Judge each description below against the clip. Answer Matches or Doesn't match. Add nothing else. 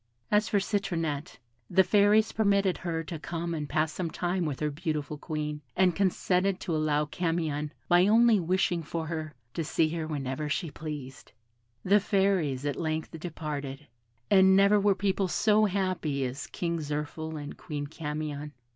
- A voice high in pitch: Doesn't match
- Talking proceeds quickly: Doesn't match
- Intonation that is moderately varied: Matches